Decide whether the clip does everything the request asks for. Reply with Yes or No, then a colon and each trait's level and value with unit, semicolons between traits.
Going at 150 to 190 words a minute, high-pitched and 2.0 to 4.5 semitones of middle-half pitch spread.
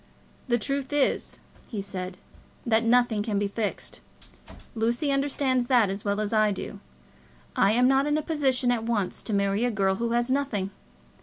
Yes: average, 175 wpm; high, 230 Hz; average, 4.1 semitones